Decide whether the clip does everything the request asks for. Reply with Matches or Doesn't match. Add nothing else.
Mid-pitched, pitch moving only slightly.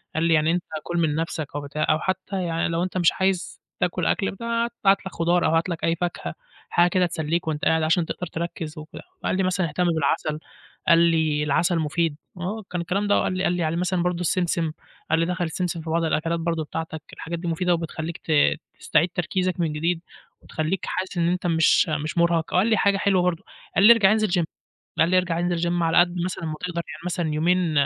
Matches